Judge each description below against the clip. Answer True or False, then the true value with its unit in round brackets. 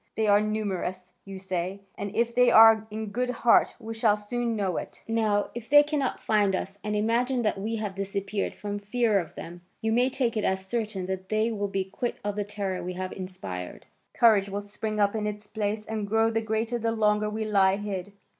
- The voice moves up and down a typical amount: False (2.2 semitones)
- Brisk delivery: True (215 wpm)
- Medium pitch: False (210 Hz)